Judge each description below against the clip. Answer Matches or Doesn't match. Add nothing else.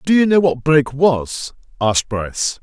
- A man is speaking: Matches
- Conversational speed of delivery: Matches